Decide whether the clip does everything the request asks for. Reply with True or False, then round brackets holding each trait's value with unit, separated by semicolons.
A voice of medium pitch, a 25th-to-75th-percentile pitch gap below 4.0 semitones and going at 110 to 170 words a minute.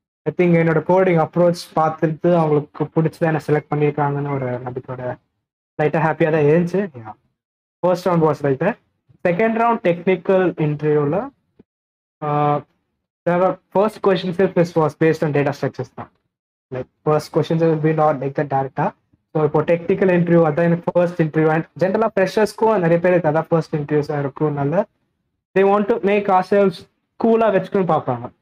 True (165 Hz; 3.6 semitones; 115 wpm)